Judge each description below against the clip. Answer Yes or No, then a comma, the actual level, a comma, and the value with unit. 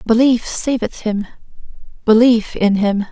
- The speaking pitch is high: Yes, high, 225 Hz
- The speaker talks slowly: Yes, slow, 115 wpm